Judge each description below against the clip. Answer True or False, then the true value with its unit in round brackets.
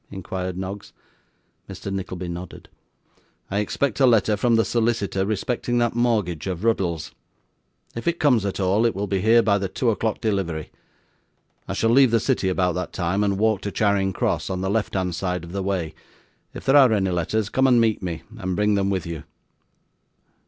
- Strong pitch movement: False (3.5 semitones)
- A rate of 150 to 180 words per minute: False (195 wpm)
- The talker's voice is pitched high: False (100 Hz)